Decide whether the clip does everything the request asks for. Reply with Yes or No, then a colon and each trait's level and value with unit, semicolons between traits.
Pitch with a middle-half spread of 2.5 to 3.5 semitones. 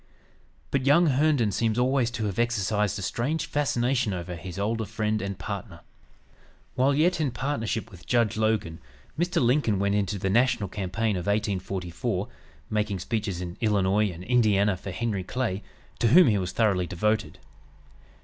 No: average, 4.0 semitones